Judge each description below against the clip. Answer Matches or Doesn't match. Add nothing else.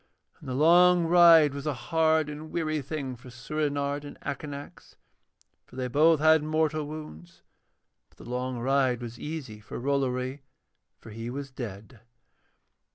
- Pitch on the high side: Doesn't match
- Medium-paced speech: Matches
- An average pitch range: Matches